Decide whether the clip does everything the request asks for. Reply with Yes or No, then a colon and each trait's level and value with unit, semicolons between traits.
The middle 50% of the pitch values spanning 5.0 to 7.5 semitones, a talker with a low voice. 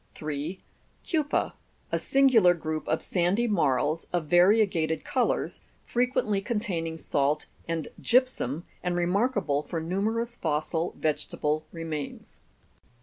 No: wide, 5.6 semitones; medium, 175 Hz